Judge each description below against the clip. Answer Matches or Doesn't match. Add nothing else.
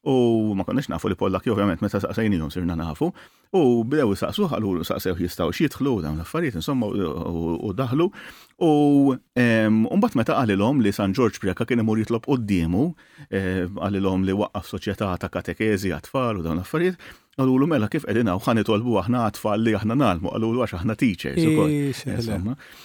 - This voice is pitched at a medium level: Doesn't match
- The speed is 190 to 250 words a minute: Doesn't match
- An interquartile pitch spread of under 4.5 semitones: Doesn't match